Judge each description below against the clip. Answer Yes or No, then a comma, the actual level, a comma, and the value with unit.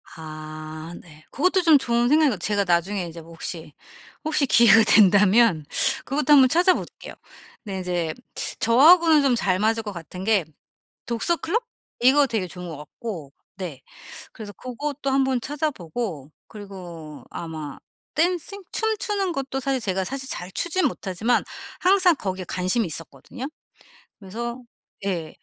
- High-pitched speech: Yes, high, 220 Hz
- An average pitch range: No, wide, 7.8 semitones